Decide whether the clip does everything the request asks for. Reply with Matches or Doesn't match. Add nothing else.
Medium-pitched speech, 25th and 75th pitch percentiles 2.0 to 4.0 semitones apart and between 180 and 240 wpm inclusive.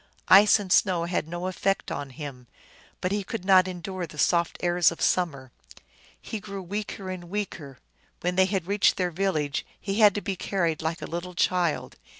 Matches